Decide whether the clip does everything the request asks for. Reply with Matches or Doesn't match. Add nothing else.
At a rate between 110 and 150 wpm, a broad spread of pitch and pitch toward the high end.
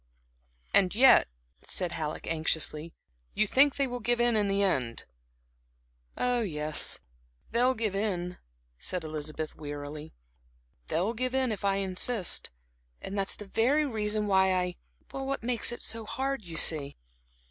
Matches